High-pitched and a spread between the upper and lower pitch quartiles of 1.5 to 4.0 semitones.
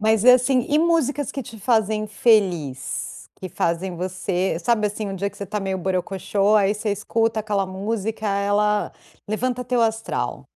Yes: high, 210 Hz; average, 2.8 semitones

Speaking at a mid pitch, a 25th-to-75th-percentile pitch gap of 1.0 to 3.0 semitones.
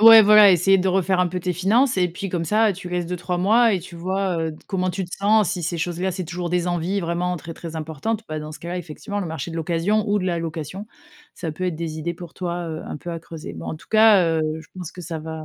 Yes: medium, 180 Hz; average, 2.7 semitones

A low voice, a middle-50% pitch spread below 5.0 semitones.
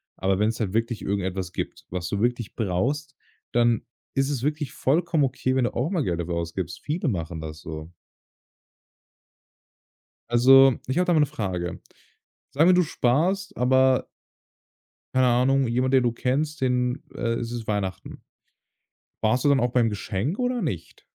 No: low, 125 Hz; wide, 5.5 semitones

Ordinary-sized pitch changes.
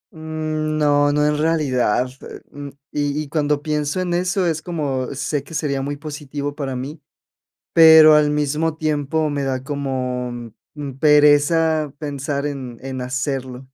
No: narrow, 2.2 semitones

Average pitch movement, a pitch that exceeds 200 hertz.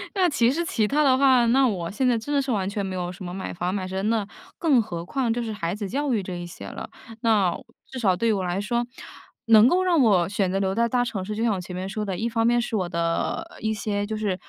Yes: average, 4.2 semitones; high, 215 Hz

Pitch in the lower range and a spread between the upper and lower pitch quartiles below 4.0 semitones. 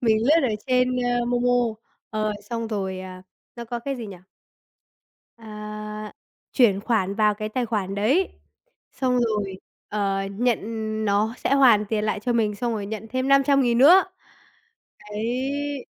No: high, 225 Hz; average, 3.0 semitones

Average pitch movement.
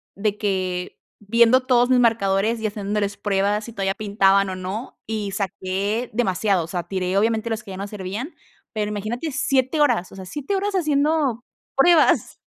Yes: average, 3.6 semitones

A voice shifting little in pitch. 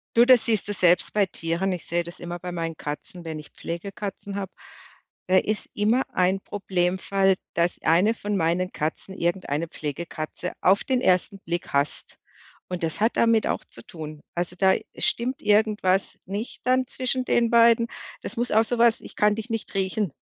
No: average, 4.1 semitones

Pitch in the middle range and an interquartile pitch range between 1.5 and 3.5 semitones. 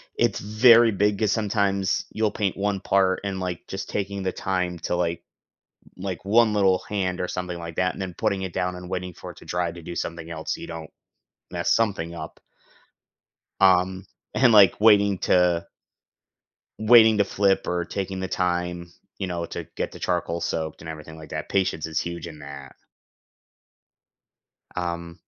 No: very low, 90 Hz; narrow, 2.6 semitones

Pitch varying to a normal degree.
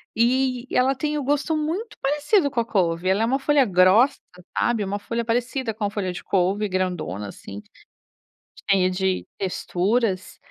No: wide, 6.2 semitones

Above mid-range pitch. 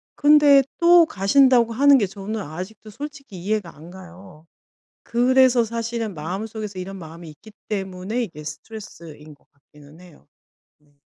Yes: high, 200 Hz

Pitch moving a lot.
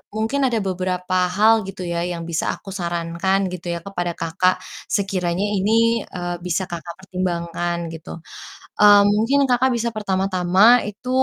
No: average, 2.9 semitones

